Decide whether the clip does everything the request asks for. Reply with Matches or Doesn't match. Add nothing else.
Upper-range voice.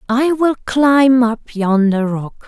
Matches